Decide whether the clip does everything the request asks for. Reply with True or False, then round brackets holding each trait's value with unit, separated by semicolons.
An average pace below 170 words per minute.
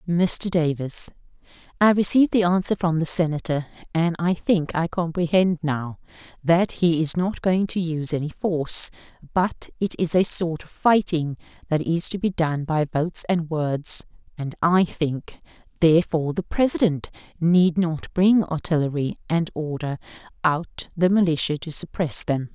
True (155 wpm)